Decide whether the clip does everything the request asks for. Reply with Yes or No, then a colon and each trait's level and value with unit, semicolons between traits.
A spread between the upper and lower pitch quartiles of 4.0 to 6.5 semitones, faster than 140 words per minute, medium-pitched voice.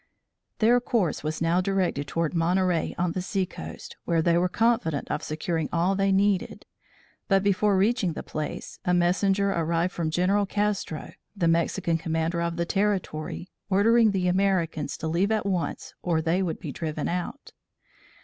No: average, 3.0 semitones; average, 165 wpm; medium, 180 Hz